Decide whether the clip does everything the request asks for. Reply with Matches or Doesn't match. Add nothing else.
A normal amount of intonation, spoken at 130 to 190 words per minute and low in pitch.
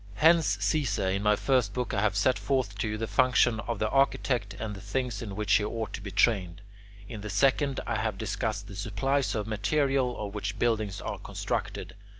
Doesn't match